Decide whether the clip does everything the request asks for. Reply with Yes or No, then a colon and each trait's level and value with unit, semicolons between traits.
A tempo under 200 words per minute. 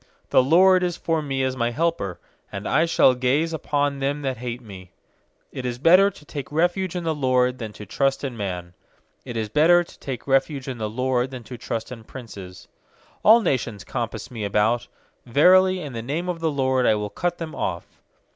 No: fast, 205 wpm